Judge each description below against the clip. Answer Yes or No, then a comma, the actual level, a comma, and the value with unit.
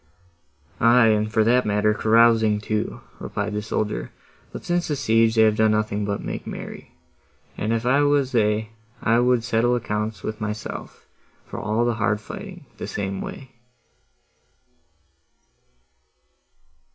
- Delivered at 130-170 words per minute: Yes, average, 140 wpm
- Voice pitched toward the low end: Yes, low, 110 Hz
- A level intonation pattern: Yes, narrow, 1.9 semitones